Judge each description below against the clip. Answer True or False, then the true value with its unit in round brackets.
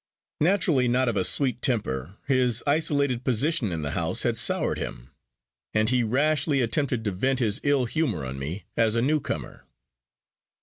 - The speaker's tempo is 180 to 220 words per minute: False (165 wpm)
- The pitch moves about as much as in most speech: True (5.0 semitones)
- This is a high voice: False (125 Hz)